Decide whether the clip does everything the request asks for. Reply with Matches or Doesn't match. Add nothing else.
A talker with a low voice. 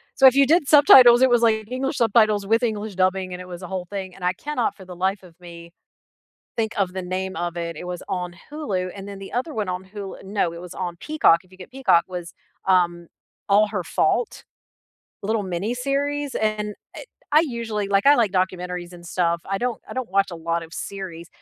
Doesn't match